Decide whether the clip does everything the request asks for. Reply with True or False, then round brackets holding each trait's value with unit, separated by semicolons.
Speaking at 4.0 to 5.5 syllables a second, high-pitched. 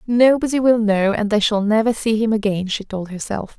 True (5.2 syllables/s; 215 Hz)